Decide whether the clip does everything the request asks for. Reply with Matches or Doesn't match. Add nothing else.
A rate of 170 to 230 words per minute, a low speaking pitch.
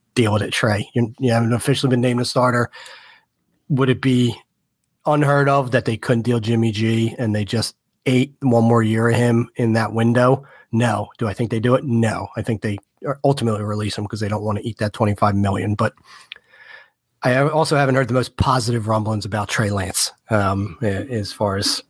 Matches